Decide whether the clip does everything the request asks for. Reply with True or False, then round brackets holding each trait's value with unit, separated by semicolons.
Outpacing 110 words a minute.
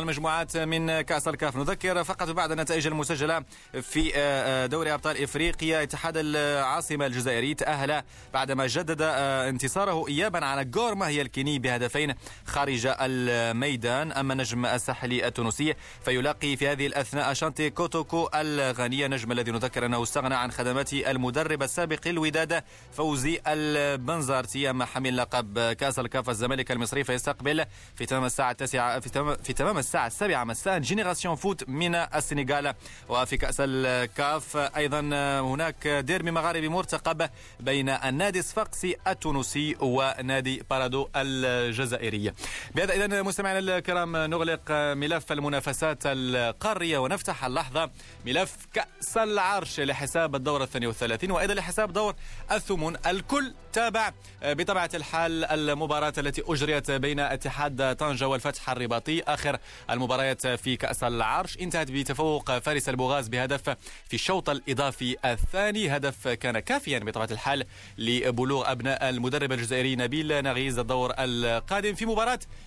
True (125 wpm)